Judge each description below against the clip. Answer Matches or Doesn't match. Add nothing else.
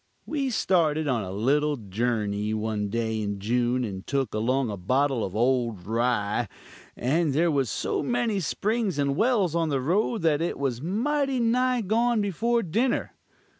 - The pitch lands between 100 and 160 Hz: Matches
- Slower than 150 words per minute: Doesn't match